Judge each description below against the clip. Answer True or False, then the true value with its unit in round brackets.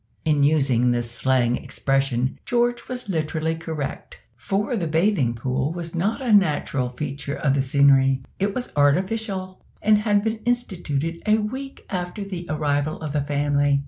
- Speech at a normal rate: True (155 wpm)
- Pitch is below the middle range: False (155 Hz)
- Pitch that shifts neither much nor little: False (6.4 semitones)